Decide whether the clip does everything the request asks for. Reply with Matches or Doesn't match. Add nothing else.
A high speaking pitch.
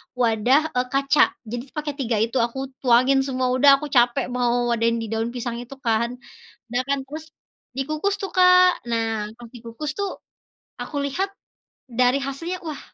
Matches